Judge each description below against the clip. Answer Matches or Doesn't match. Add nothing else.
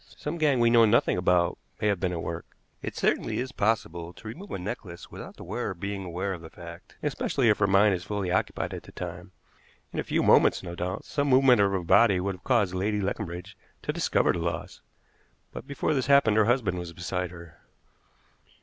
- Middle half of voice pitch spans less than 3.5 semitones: Doesn't match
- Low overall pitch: Matches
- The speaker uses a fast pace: Matches